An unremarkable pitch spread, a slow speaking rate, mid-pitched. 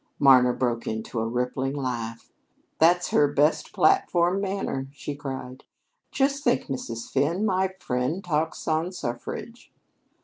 No: wide, 6.0 semitones; slow, 130 wpm; medium, 145 Hz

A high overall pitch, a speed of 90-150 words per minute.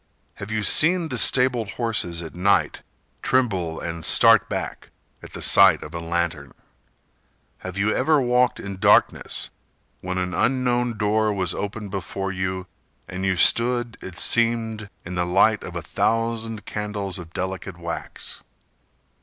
No: low, 100 Hz; average, 145 wpm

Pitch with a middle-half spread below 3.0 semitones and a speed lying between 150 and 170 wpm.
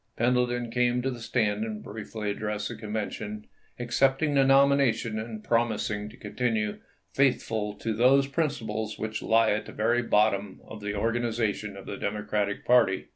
Yes: narrow, 2.5 semitones; average, 160 wpm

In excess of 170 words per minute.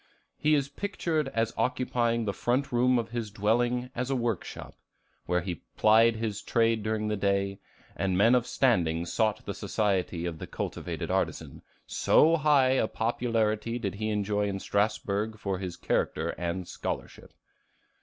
No: average, 160 wpm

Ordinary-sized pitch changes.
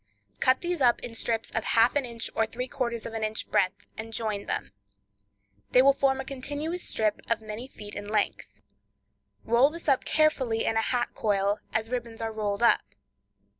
Yes: average, 3.0 semitones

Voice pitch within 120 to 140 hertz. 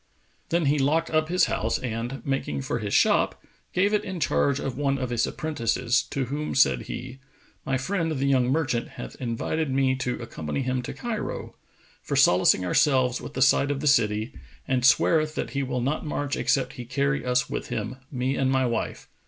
Yes: low, 135 Hz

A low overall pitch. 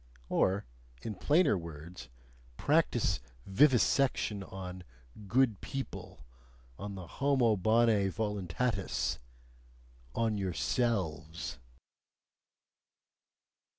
Yes: low, 100 Hz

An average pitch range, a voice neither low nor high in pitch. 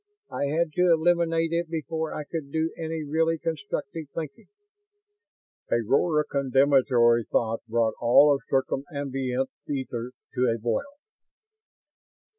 Yes: average, 4.2 semitones; medium, 145 Hz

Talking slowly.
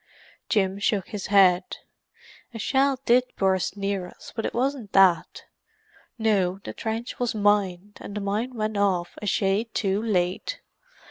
No: average, 150 wpm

